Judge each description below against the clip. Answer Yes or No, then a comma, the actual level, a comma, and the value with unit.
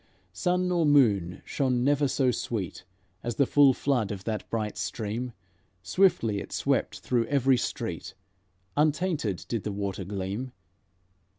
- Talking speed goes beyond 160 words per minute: No, slow, 135 wpm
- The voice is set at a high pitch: No, low, 120 Hz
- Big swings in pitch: Yes, wide, 5.7 semitones